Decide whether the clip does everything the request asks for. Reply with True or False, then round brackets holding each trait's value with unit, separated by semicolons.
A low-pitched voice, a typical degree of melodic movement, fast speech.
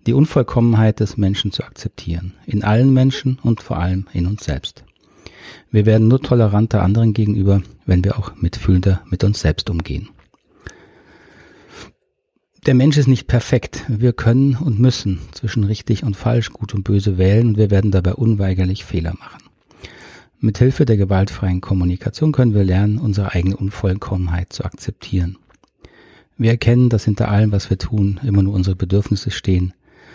False (105 Hz; 3.5 semitones; 155 wpm)